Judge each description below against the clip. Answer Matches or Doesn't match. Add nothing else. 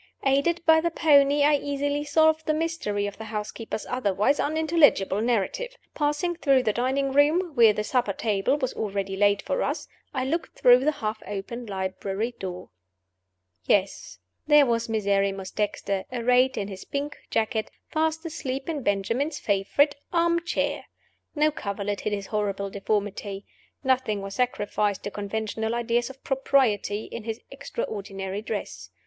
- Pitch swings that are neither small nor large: Doesn't match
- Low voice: Doesn't match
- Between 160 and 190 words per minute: Doesn't match